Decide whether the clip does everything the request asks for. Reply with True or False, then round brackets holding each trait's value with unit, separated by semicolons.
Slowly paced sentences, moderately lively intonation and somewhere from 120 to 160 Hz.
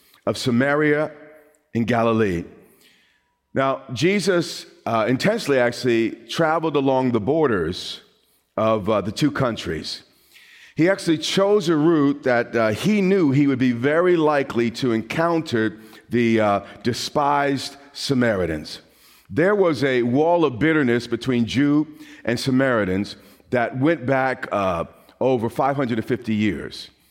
True (120 wpm; 4.6 semitones; 135 Hz)